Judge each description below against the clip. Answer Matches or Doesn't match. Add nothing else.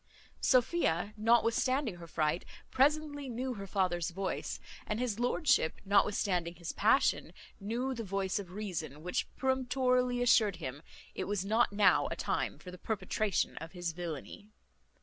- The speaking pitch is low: Doesn't match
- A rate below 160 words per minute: Matches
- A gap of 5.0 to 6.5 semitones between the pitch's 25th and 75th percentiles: Matches